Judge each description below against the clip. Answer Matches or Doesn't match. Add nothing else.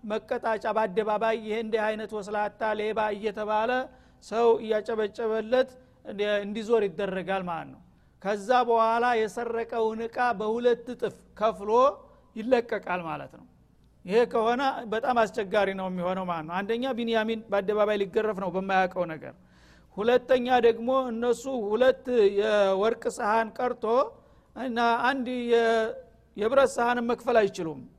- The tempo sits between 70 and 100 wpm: Doesn't match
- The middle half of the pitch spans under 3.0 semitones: Matches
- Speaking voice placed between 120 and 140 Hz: Doesn't match